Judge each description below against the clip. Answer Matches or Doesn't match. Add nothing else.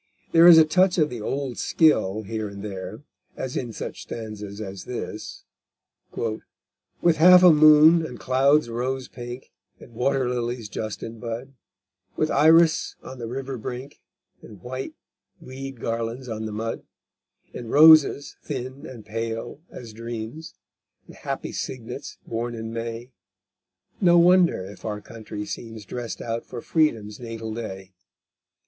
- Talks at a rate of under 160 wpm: Matches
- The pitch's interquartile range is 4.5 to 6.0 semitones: Doesn't match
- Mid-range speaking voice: Doesn't match